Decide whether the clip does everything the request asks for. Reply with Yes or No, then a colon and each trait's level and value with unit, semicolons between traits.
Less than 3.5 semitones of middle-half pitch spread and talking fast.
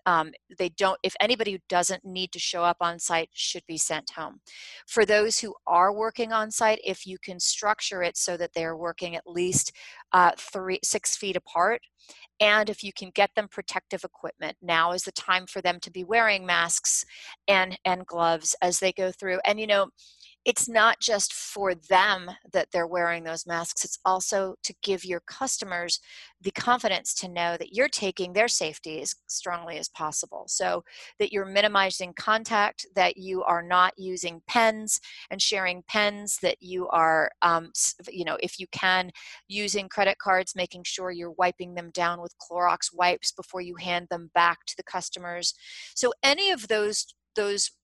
No: average, 2.9 semitones; average, 180 wpm